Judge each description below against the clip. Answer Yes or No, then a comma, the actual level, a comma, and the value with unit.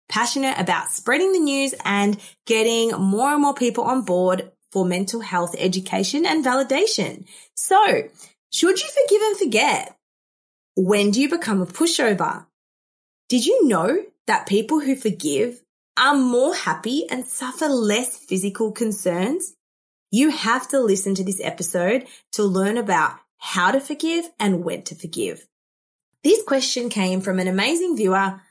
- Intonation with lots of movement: Yes, wide, 7.2 semitones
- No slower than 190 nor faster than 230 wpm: No, average, 145 wpm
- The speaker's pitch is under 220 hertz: No, high, 235 Hz